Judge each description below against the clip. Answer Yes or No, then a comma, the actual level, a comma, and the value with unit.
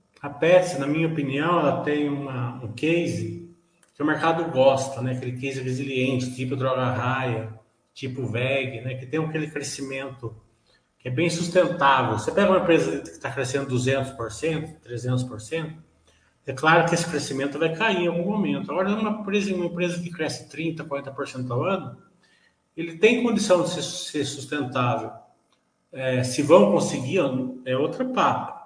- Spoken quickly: No, average, 160 wpm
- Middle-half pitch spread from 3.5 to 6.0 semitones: Yes, average, 4.6 semitones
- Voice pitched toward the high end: No, medium, 140 Hz